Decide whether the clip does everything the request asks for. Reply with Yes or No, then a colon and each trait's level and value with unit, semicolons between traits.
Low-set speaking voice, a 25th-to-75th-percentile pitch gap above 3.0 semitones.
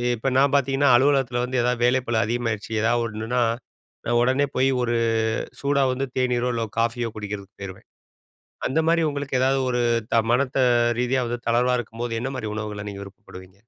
No: low, 120 Hz; narrow, 2.5 semitones